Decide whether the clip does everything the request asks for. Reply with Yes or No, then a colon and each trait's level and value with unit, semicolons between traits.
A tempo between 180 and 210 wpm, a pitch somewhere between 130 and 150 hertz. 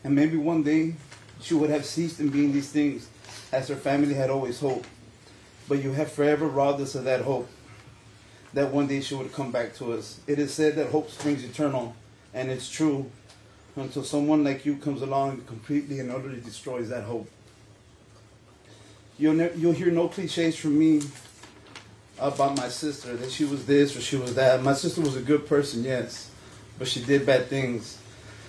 Yes: average, 190 wpm; low, 135 Hz